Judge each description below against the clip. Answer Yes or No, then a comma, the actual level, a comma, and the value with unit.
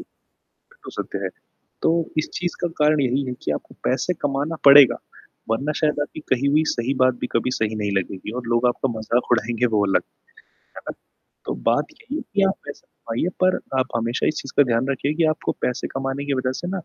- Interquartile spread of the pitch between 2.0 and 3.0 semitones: No, average, 4.0 semitones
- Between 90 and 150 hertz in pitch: Yes, low, 135 Hz